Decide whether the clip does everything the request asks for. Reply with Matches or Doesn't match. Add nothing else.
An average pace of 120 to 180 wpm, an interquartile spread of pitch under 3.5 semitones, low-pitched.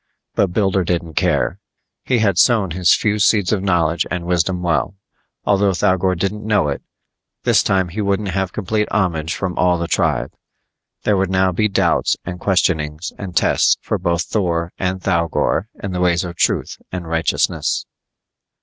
Matches